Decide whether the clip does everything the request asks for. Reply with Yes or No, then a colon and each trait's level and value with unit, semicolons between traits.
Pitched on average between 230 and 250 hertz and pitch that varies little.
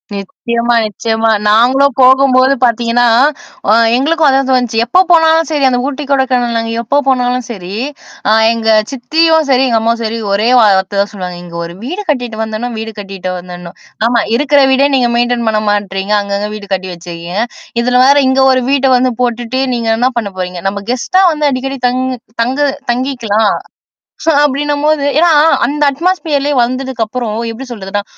No: high, 245 Hz; average, 3.9 semitones